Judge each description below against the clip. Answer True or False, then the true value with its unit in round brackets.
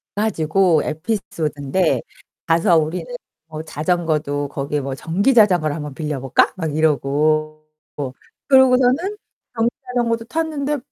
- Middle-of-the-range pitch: True (160 Hz)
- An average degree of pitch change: False (7.0 semitones)